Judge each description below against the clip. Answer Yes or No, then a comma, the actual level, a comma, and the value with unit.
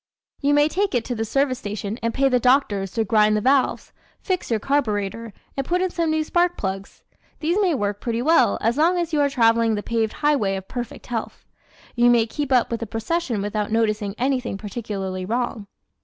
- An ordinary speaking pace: No, fast, 210 wpm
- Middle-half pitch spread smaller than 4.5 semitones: No, average, 5.0 semitones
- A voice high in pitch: Yes, high, 235 Hz